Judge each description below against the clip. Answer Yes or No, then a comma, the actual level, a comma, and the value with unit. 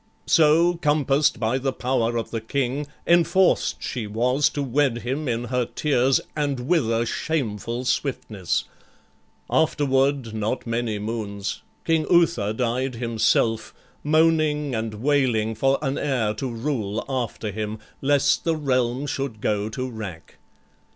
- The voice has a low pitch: Yes, low, 125 Hz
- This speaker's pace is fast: No, slow, 135 wpm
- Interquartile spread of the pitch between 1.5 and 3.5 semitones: No, average, 4.3 semitones